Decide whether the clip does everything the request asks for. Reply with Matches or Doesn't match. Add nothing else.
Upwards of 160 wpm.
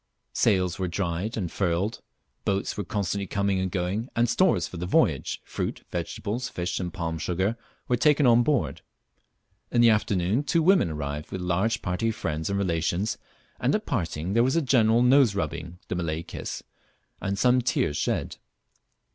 Matches